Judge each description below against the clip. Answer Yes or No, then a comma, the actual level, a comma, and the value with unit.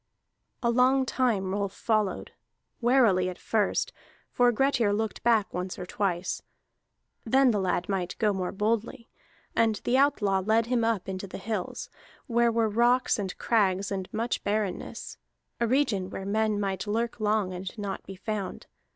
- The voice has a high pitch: Yes, high, 215 Hz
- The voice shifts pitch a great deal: No, average, 3.4 semitones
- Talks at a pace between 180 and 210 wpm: No, average, 160 wpm